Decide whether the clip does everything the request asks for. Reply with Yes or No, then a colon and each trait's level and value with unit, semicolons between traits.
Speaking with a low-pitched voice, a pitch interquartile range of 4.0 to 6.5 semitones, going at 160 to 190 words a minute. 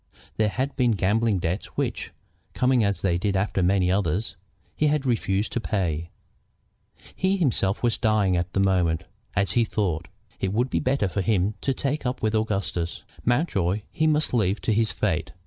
Yes: low, 105 Hz; average, 4.4 semitones; average, 180 wpm